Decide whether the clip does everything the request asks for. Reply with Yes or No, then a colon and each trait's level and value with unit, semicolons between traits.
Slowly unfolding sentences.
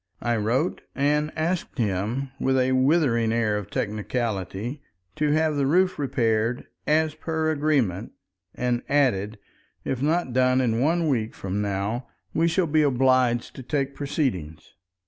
No: average, 145 wpm